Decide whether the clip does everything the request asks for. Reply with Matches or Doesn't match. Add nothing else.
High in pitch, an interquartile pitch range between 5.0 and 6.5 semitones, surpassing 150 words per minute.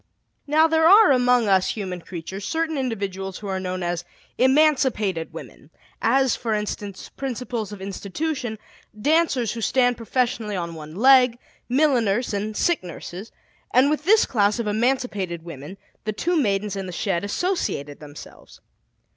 Doesn't match